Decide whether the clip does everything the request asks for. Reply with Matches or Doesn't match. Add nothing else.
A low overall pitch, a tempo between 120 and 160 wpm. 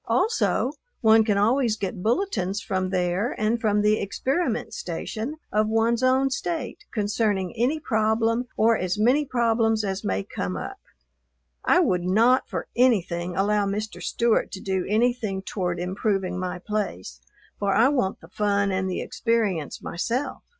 Doesn't match